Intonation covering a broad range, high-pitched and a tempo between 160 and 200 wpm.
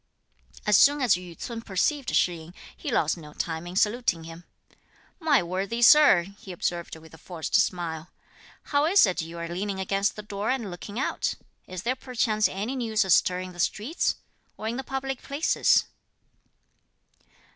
Yes: wide, 5.7 semitones; high, 200 Hz; average, 170 wpm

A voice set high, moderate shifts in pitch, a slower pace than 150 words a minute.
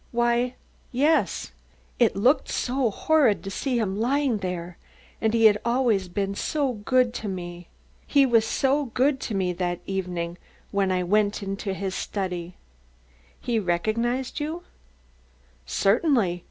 Yes: high, 215 Hz; average, 5.0 semitones; average, 140 wpm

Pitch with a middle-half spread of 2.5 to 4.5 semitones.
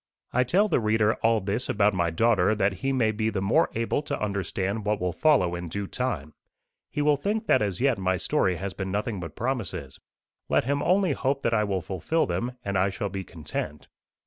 No: average, 5.2 semitones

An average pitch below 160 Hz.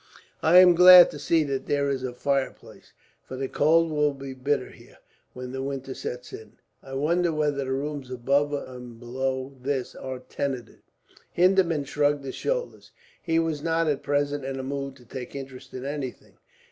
Yes: medium, 140 Hz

